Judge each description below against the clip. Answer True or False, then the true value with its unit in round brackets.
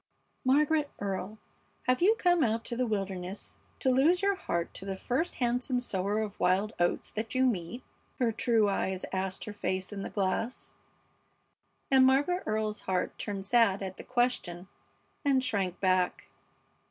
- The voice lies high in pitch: True (220 Hz)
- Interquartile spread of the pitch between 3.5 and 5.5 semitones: True (5.1 semitones)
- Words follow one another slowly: False (160 wpm)